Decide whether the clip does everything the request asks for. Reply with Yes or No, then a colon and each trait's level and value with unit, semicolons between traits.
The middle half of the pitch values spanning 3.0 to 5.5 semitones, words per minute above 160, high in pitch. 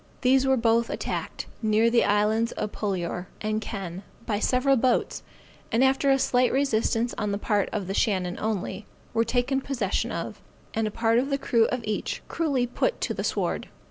Yes: average, 3.3 semitones; average, 185 wpm; high, 230 Hz